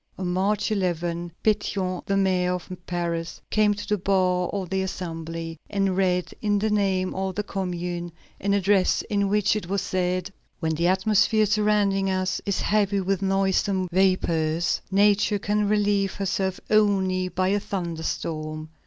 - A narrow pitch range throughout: Yes, narrow, 2.1 semitones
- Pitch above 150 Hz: Yes, high, 190 Hz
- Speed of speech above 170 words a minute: No, average, 155 wpm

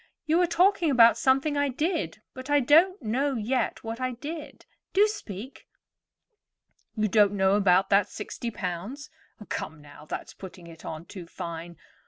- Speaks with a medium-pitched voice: No, high, 235 Hz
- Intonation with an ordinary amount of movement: No, wide, 7.4 semitones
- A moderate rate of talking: Yes, average, 160 wpm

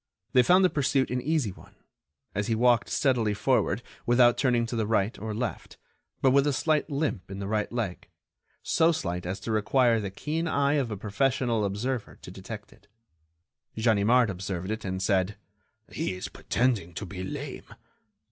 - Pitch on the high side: No, low, 115 Hz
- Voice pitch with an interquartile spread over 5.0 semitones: No, average, 4.7 semitones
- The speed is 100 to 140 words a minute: No, average, 175 wpm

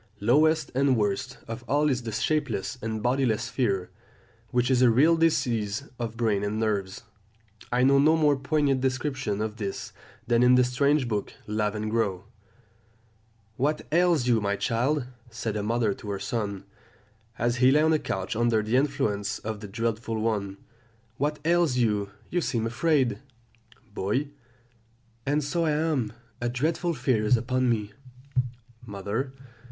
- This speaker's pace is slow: No, average, 155 wpm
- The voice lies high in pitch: No, low, 120 Hz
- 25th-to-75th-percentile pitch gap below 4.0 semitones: No, average, 4.5 semitones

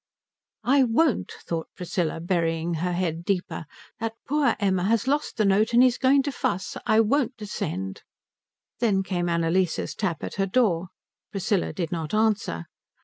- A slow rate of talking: No, average, 155 wpm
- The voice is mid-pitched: No, high, 195 Hz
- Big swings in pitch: No, average, 5.0 semitones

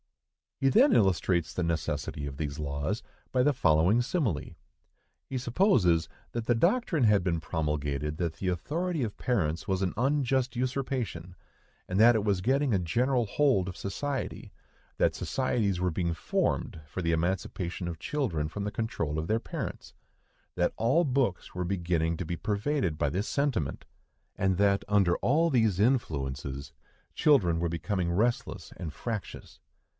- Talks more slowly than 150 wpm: No, average, 155 wpm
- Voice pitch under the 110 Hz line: Yes, low, 100 Hz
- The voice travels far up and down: Yes, wide, 7.1 semitones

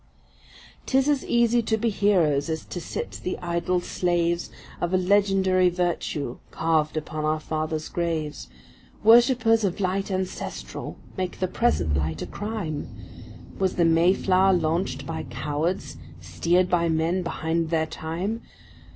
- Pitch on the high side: No, medium, 175 Hz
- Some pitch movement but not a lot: Yes, average, 3.4 semitones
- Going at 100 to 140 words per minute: Yes, slow, 135 wpm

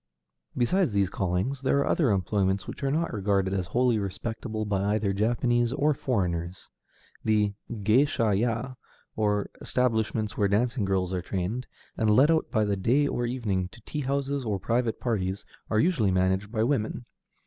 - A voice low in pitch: Yes, low, 110 Hz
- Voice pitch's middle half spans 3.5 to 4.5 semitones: Yes, average, 4.2 semitones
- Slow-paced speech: No, average, 165 wpm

